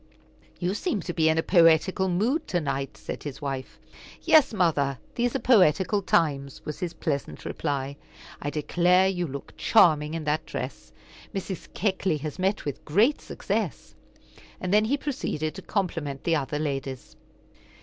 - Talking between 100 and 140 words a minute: No, average, 160 wpm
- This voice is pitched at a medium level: Yes, medium, 165 Hz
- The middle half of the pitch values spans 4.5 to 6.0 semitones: Yes, average, 4.8 semitones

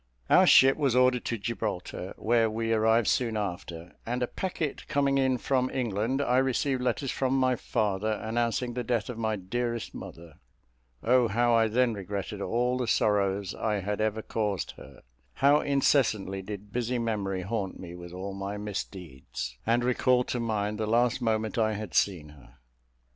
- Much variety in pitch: No, average, 3.7 semitones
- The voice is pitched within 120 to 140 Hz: No, low, 110 Hz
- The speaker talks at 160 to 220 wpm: Yes, average, 170 wpm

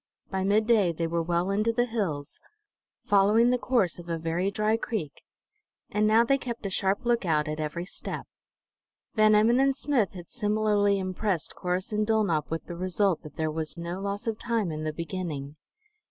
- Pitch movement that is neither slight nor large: Yes, average, 4.3 semitones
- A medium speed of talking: Yes, average, 185 wpm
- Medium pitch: No, high, 195 Hz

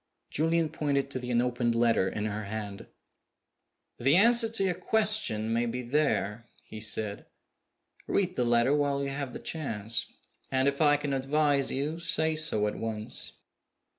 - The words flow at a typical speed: Yes, average, 160 wpm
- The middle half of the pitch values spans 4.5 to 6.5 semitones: Yes, average, 5.2 semitones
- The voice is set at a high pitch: No, low, 135 Hz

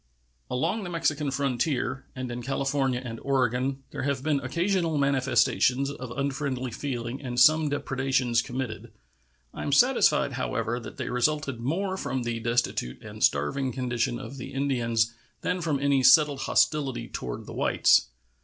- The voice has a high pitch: No, low, 135 Hz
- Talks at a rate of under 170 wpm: Yes, average, 150 wpm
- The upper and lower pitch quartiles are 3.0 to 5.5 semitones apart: No, narrow, 2.6 semitones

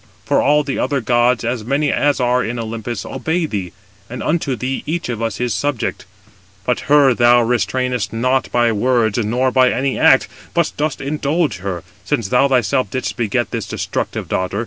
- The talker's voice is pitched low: Yes, low, 125 Hz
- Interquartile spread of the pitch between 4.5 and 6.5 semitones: No, average, 3.2 semitones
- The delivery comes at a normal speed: Yes, average, 180 wpm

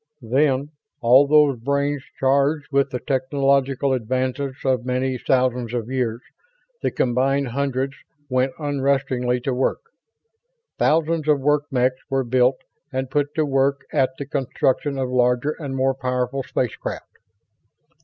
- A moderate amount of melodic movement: No, narrow, 1.7 semitones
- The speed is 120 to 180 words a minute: Yes, slow, 135 wpm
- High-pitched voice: No, low, 135 Hz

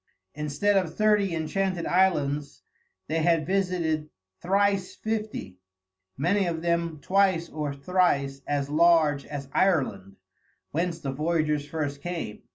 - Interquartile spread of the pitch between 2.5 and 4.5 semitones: Yes, average, 4.2 semitones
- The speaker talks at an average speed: No, slow, 120 wpm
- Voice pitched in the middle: Yes, medium, 165 Hz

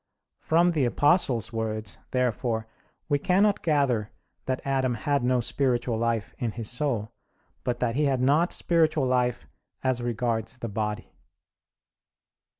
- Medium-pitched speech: No, low, 125 Hz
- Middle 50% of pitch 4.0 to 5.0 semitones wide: No, average, 3.6 semitones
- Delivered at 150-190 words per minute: No, slow, 135 wpm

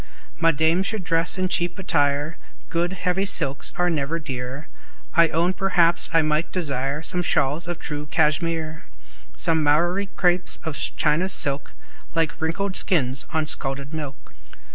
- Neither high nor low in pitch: Yes, medium, 165 Hz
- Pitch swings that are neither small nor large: Yes, average, 3.1 semitones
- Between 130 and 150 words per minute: Yes, average, 145 wpm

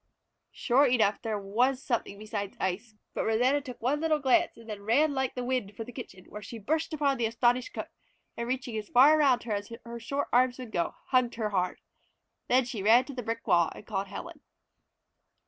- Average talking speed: No, fast, 210 wpm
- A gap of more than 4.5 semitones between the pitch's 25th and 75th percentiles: No, average, 3.5 semitones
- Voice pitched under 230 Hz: No, high, 240 Hz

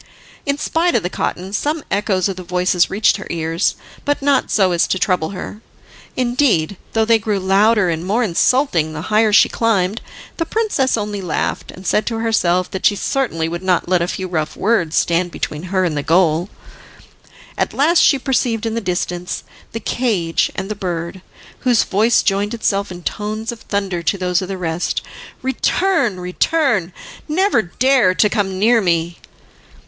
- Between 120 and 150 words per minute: No, average, 180 wpm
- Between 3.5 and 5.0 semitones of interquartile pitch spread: Yes, average, 4.4 semitones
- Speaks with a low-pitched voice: No, high, 195 Hz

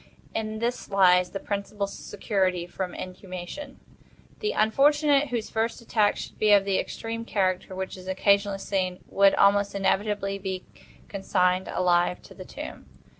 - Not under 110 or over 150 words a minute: Yes, average, 145 wpm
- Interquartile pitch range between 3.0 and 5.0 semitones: No, narrow, 2.6 semitones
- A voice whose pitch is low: No, high, 200 Hz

